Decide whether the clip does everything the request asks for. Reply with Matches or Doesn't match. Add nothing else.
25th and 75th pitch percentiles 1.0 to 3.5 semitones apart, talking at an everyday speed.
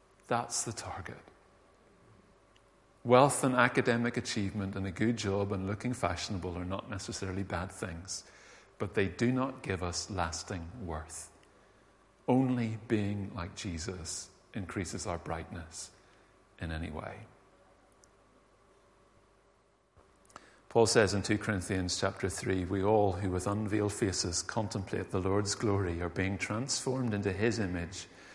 Doesn't match